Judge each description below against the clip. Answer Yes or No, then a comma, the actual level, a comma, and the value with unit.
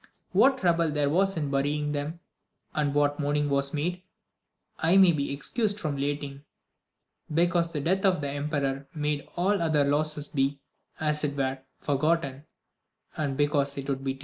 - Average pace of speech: Yes, average, 170 wpm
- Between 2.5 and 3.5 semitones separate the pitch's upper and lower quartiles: Yes, average, 2.8 semitones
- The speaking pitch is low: No, medium, 150 Hz